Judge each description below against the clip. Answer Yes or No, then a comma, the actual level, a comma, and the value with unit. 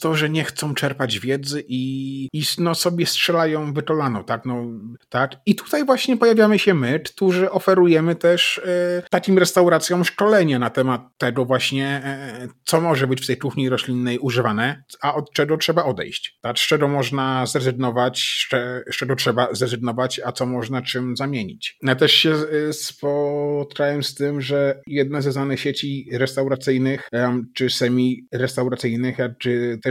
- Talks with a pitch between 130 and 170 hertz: Yes, low, 135 Hz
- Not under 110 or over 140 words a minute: No, average, 155 wpm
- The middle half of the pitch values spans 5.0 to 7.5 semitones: No, average, 3.5 semitones